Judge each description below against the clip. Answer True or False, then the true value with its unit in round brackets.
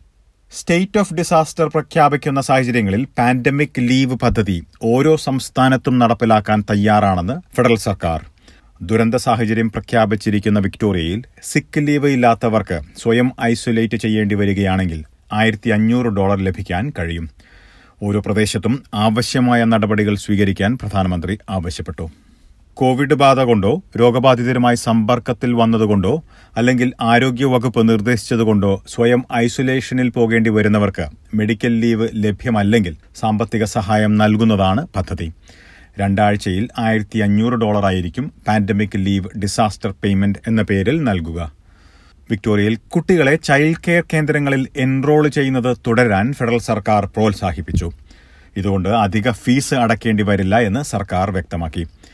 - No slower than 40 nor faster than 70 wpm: False (100 wpm)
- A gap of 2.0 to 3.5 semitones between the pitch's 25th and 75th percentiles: False (4.1 semitones)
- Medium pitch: False (110 Hz)